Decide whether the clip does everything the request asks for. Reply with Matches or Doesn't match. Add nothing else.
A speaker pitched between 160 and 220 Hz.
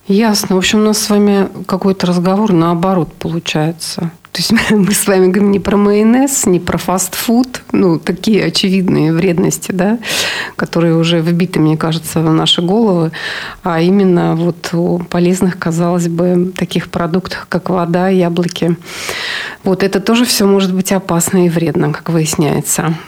Matches